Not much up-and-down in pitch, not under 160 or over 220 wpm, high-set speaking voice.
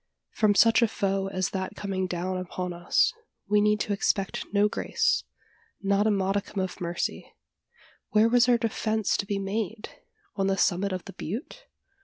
Yes: narrow, 2.3 semitones; average, 165 wpm; high, 200 Hz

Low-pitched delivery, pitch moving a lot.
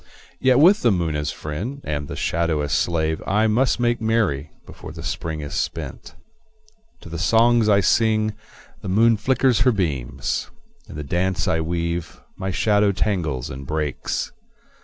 Yes: very low, 90 Hz; wide, 6.1 semitones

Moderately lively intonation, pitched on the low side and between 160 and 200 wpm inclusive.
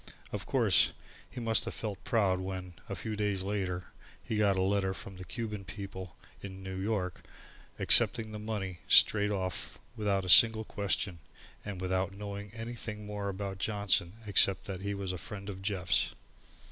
No: narrow, 1.8 semitones; low, 100 Hz; average, 170 wpm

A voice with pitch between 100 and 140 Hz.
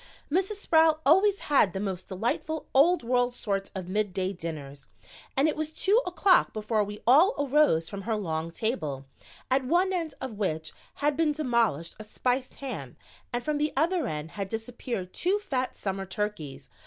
No: high, 240 Hz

